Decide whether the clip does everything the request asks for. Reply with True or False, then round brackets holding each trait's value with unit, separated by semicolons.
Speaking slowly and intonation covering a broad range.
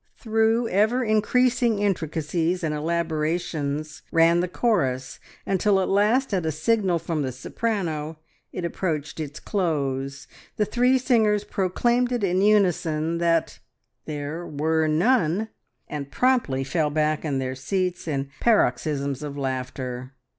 True (125 wpm; 5.9 semitones)